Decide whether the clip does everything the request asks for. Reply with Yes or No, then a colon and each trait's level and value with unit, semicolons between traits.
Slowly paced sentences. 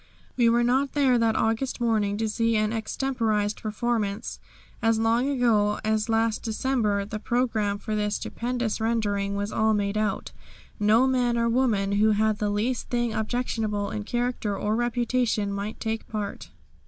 No: average, 160 wpm